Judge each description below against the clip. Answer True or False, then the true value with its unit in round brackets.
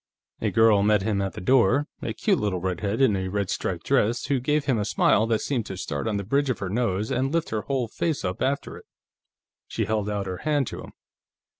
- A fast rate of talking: True (240 wpm)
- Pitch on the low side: True (110 Hz)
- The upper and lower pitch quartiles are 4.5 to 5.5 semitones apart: True (4.9 semitones)